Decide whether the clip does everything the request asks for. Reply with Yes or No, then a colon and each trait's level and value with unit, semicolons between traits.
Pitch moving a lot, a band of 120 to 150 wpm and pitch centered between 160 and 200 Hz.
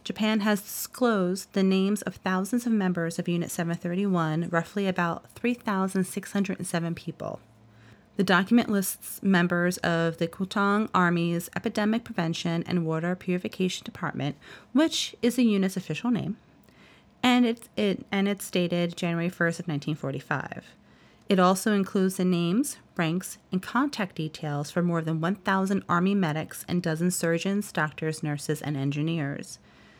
No: average, 3.1 semitones; average, 140 wpm; medium, 185 Hz